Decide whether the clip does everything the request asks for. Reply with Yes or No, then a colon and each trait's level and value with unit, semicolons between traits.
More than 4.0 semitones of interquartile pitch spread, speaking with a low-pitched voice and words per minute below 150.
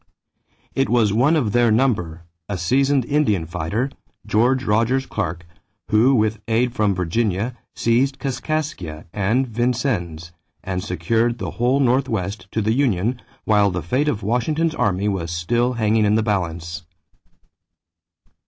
Yes: average, 5.1 semitones; low, 110 Hz; slow, 135 wpm